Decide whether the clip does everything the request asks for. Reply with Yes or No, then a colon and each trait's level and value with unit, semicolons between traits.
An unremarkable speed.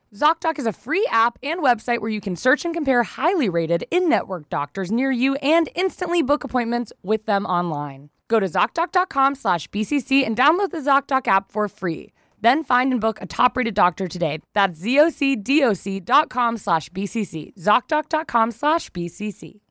Yes: average, 145 wpm